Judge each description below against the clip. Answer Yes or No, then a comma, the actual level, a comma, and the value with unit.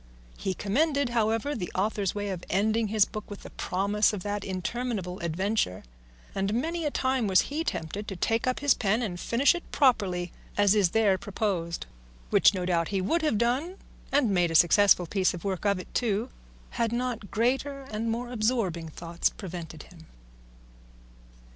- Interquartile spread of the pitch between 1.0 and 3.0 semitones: No, average, 4.4 semitones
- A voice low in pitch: No, high, 205 Hz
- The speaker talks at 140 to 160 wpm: No, average, 175 wpm